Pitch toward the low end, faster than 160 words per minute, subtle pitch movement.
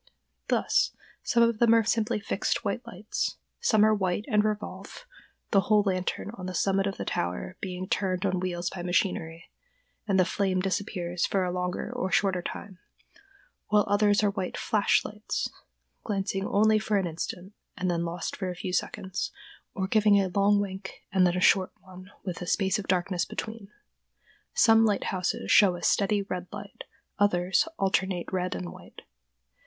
No: high, 195 Hz; average, 170 wpm; narrow, 2.3 semitones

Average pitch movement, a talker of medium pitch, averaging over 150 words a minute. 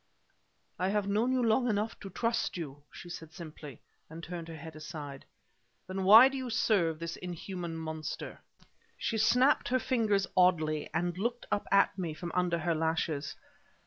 Yes: average, 5.0 semitones; medium, 180 Hz; average, 170 wpm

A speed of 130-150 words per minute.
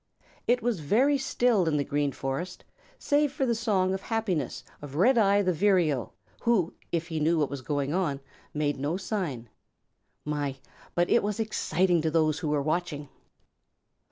No: average, 165 wpm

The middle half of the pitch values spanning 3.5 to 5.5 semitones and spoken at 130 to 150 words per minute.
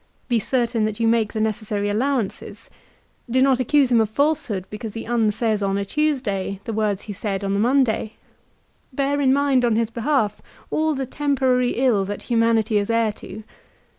No: average, 3.8 semitones; average, 180 wpm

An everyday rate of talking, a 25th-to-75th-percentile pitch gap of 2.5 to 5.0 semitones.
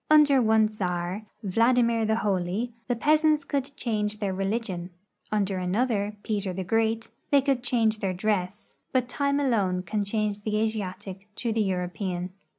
Yes: average, 160 wpm; average, 3.7 semitones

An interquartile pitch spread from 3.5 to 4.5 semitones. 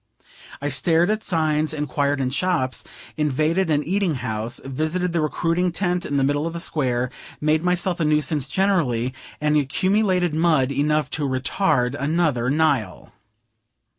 Yes: average, 4.0 semitones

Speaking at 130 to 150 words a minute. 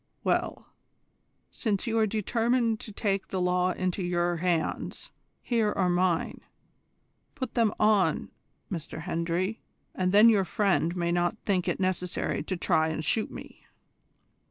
Yes: average, 140 wpm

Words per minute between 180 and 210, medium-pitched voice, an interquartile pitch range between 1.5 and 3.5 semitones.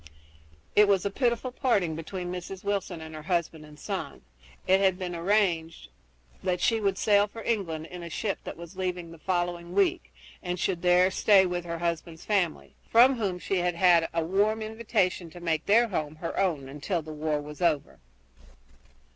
Yes: average, 185 wpm; medium, 180 Hz; average, 3.2 semitones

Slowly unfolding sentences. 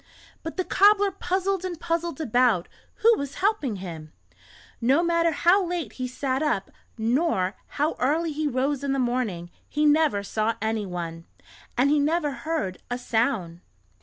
No: average, 155 wpm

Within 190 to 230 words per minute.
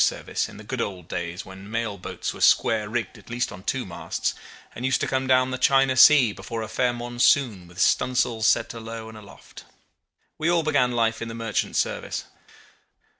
Yes: average, 200 wpm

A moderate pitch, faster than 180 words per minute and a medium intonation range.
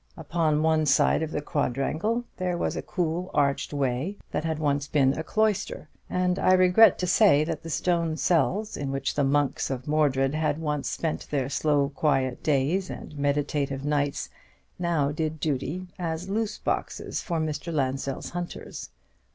No: medium, 155 Hz; average, 165 wpm; average, 3.5 semitones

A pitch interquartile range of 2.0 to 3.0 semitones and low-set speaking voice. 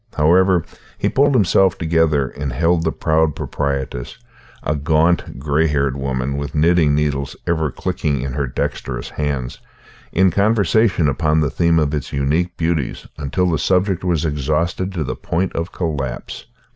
No: average, 3.4 semitones; very low, 80 Hz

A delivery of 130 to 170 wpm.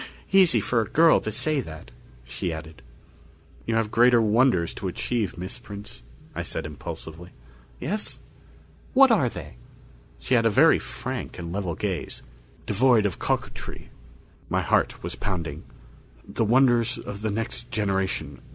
Yes: average, 145 wpm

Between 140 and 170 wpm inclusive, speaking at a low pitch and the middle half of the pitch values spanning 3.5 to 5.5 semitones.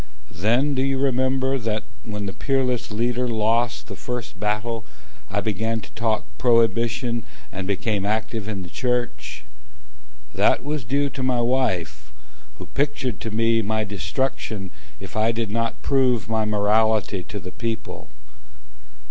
No: average, 145 wpm; low, 115 Hz; average, 2.9 semitones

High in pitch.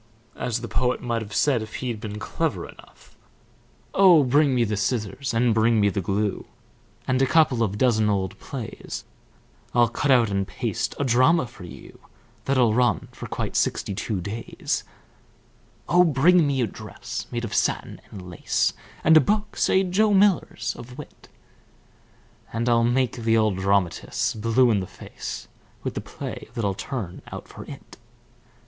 No: low, 120 Hz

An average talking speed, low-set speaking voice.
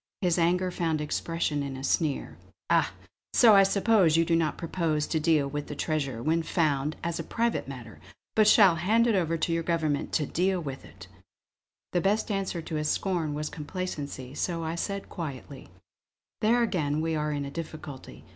No: average, 185 wpm; medium, 165 Hz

